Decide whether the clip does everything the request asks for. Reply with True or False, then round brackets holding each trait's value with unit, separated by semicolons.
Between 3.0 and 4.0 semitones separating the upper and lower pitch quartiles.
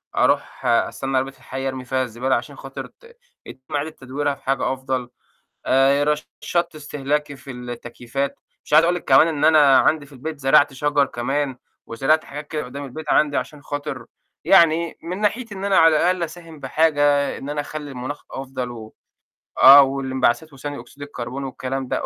False (2.6 semitones)